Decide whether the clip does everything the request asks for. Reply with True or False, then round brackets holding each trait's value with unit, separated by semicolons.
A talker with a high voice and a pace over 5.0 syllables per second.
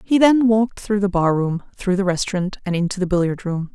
True (195 Hz; 5.8 syllables/s)